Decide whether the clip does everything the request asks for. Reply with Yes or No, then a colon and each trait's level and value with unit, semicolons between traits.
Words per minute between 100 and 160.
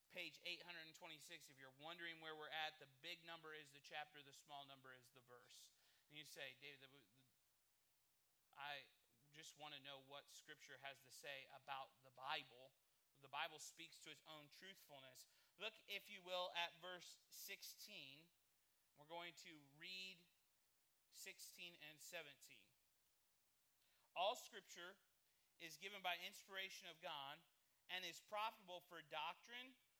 Yes: average, 145 wpm